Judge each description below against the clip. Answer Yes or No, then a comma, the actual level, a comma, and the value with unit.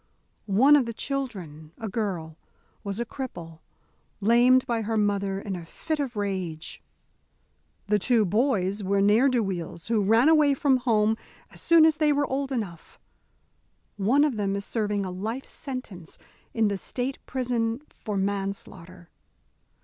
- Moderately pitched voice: No, high, 215 Hz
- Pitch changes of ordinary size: Yes, average, 4.7 semitones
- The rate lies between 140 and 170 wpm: Yes, average, 155 wpm